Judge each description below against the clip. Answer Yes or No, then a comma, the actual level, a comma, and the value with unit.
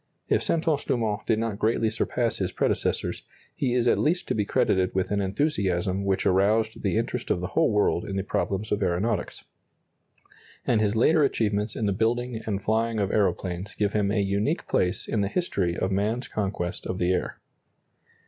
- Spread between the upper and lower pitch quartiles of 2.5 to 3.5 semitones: Yes, average, 2.8 semitones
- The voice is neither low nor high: No, low, 105 Hz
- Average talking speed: Yes, average, 185 wpm